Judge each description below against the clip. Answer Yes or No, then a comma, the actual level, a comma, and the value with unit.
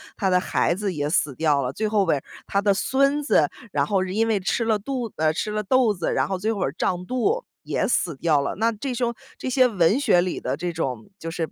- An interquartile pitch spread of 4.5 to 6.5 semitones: Yes, wide, 5.5 semitones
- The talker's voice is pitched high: Yes, high, 195 Hz